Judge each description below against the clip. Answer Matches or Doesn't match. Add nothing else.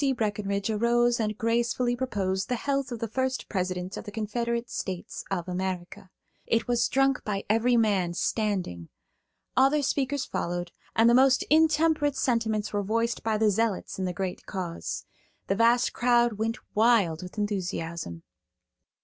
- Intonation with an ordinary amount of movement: Matches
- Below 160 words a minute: Matches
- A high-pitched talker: Matches